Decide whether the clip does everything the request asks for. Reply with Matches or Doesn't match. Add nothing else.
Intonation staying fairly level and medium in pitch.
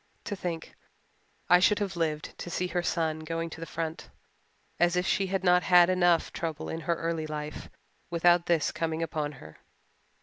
Matches